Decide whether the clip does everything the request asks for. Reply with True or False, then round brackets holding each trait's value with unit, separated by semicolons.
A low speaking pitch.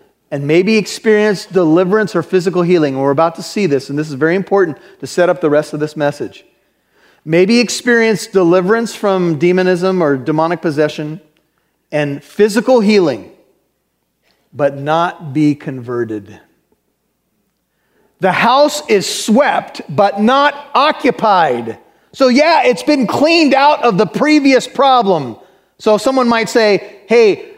False (190 Hz)